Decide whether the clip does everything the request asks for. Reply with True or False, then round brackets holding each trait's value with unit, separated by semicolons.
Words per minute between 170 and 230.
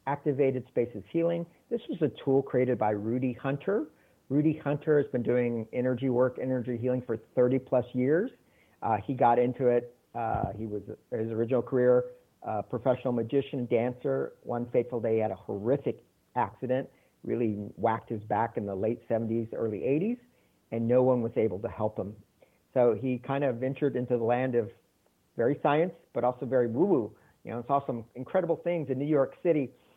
True (185 wpm)